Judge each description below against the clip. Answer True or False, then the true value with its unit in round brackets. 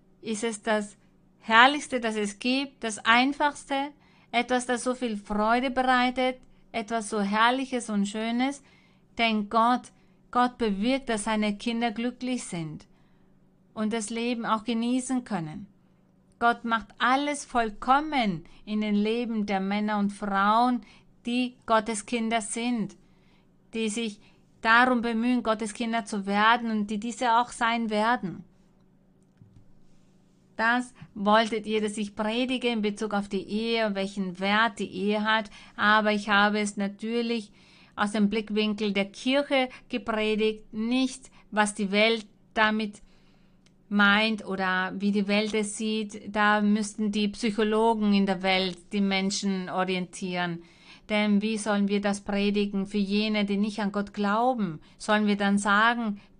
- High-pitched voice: True (215 Hz)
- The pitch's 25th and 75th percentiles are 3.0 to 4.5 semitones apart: False (2.5 semitones)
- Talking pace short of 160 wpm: True (140 wpm)